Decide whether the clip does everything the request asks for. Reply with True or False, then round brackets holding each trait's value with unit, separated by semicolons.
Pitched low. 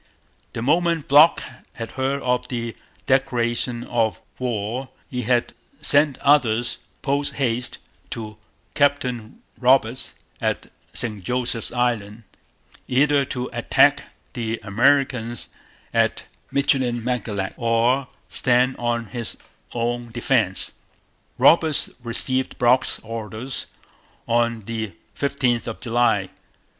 True (120 Hz)